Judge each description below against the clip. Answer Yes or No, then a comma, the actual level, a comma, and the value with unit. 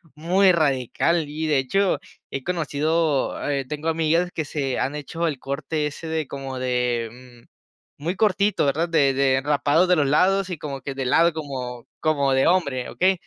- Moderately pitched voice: Yes, medium, 150 Hz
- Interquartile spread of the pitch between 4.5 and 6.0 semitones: No, average, 3.7 semitones